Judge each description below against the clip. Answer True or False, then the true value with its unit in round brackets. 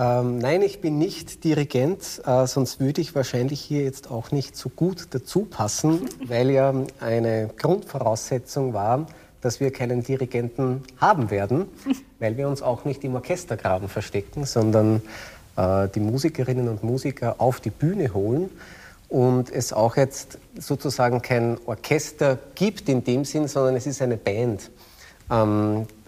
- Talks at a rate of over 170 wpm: False (140 wpm)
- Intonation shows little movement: False (3.6 semitones)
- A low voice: True (130 Hz)